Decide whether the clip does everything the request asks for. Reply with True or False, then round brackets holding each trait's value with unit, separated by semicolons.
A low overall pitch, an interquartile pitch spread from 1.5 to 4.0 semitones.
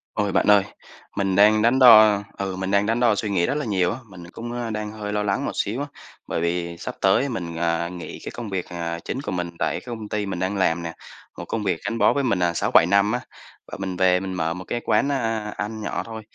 True (100 Hz; 3.7 semitones)